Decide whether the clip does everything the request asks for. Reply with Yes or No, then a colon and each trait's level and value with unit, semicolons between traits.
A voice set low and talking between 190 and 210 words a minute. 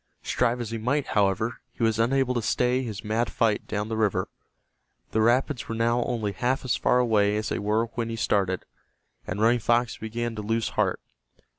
Yes: low, 115 Hz; average, 195 wpm